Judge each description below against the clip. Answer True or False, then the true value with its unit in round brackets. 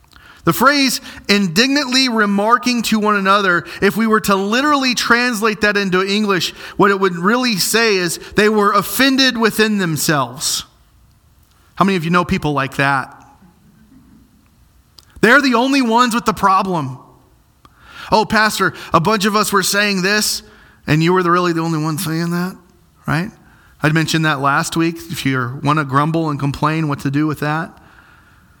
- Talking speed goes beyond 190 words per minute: False (165 wpm)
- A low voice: False (195 Hz)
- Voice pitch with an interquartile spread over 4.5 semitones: True (5.2 semitones)